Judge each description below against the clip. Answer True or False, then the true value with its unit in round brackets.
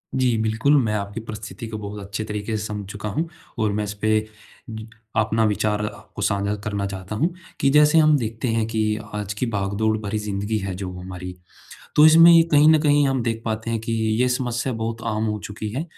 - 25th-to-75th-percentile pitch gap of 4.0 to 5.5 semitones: False (2.8 semitones)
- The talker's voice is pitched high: False (110 Hz)